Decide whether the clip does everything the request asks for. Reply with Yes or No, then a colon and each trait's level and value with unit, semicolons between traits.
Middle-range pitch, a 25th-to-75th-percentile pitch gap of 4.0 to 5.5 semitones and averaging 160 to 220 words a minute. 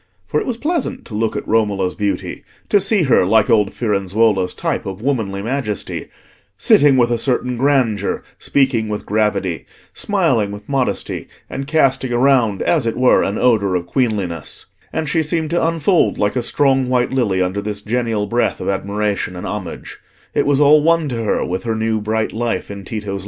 No: low, 115 Hz; average, 4.9 semitones; average, 185 wpm